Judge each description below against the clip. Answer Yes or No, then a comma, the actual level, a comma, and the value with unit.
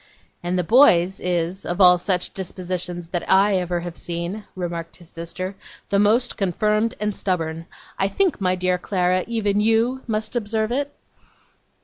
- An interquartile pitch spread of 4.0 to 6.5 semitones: No, average, 3.3 semitones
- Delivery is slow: No, average, 155 wpm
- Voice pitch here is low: No, medium, 185 Hz